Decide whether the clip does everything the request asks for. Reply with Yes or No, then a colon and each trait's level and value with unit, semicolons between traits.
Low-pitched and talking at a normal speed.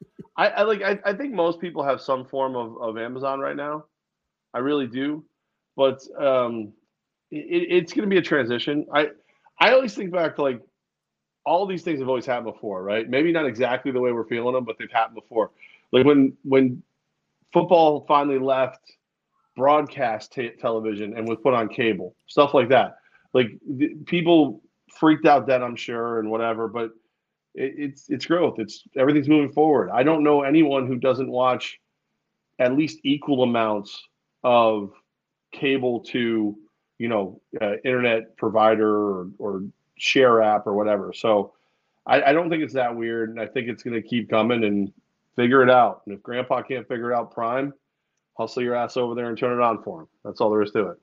Yes: low, 125 Hz; average, 185 wpm